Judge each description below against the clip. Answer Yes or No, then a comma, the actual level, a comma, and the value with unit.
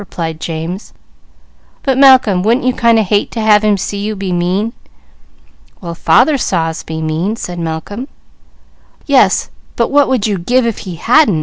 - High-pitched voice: Yes, high, 205 Hz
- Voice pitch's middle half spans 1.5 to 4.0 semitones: No, average, 5.2 semitones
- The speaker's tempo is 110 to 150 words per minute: No, average, 175 wpm